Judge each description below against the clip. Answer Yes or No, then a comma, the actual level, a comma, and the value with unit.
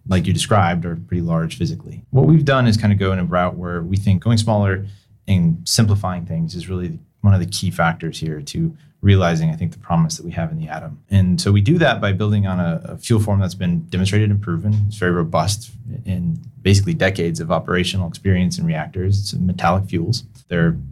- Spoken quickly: Yes, fast, 220 wpm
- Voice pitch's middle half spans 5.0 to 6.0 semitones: No, average, 3.6 semitones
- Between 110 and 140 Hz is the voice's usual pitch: No, very low, 95 Hz